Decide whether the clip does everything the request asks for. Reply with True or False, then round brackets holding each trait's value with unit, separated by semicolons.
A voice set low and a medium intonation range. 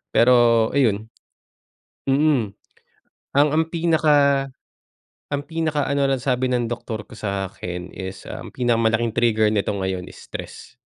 True (120 Hz; 4.5 semitones)